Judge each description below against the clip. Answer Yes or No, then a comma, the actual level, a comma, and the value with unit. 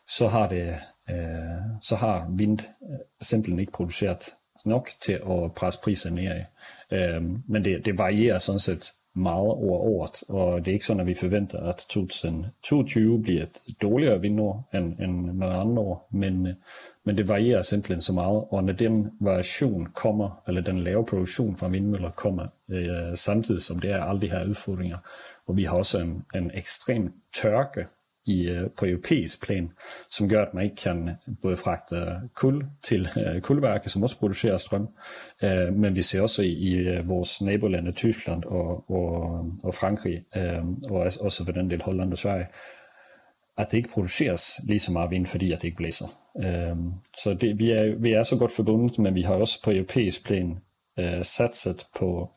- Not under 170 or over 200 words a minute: Yes, average, 175 wpm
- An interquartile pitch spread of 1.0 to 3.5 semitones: Yes, average, 3.0 semitones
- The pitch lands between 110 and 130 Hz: No, very low, 95 Hz